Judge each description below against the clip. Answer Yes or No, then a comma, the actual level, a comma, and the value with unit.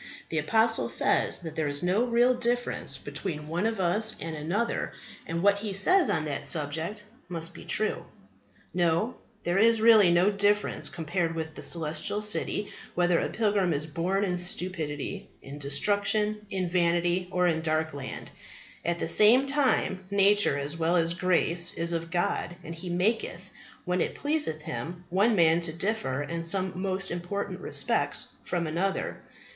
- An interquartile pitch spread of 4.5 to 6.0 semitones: No, average, 3.9 semitones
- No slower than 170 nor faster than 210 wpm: No, average, 160 wpm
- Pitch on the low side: No, medium, 175 Hz